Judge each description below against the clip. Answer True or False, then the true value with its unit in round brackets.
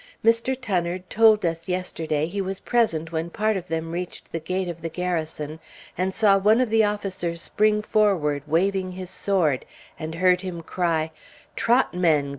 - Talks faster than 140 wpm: True (170 wpm)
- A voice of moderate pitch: True (180 Hz)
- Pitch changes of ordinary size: True (3.8 semitones)